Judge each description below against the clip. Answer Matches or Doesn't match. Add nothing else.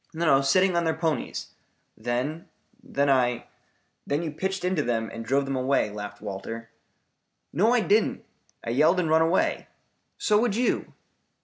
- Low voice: Doesn't match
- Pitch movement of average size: Doesn't match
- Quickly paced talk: Doesn't match